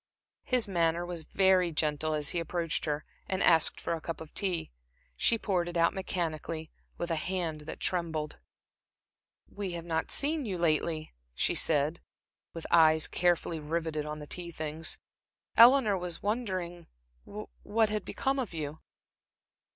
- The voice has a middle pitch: Yes, medium, 170 Hz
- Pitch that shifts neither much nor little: Yes, average, 3.0 semitones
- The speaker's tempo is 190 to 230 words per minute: No, average, 150 wpm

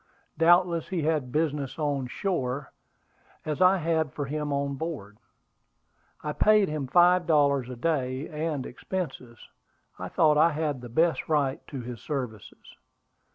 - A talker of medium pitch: Yes, medium, 150 Hz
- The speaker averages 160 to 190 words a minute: No, average, 150 wpm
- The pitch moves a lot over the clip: No, average, 3.6 semitones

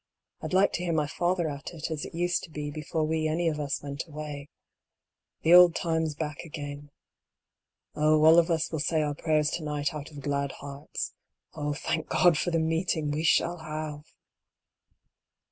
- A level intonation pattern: Yes, narrow, 1.9 semitones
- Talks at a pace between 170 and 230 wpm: Yes, average, 195 wpm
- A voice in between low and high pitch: Yes, medium, 155 Hz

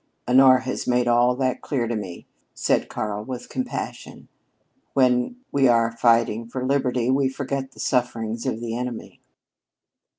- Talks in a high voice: No, low, 125 Hz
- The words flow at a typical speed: Yes, average, 145 wpm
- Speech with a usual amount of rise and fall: No, narrow, 2.2 semitones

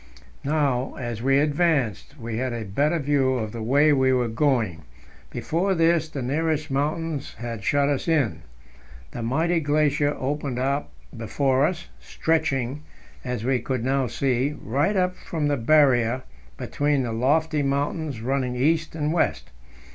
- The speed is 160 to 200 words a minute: No, average, 150 wpm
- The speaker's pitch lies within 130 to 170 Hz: Yes, medium, 140 Hz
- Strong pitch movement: No, average, 3.5 semitones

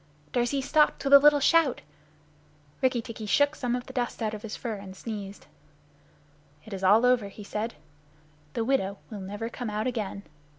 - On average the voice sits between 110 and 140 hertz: No, high, 230 Hz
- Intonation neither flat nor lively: Yes, average, 3.7 semitones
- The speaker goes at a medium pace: Yes, average, 180 wpm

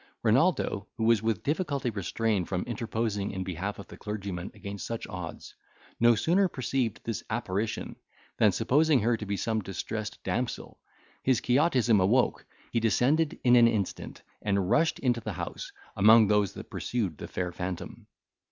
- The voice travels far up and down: No, average, 3.5 semitones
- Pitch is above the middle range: No, low, 110 Hz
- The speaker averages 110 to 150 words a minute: No, average, 160 wpm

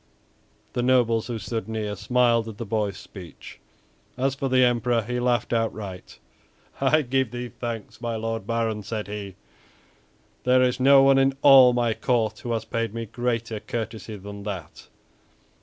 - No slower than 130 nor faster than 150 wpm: No, average, 160 wpm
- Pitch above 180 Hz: No, low, 115 Hz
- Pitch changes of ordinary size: No, narrow, 2.3 semitones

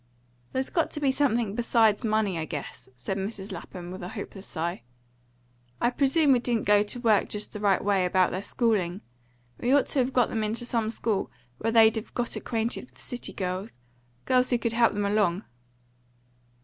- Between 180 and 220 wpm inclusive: Yes, average, 190 wpm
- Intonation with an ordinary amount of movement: Yes, average, 3.8 semitones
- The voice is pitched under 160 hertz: No, high, 220 Hz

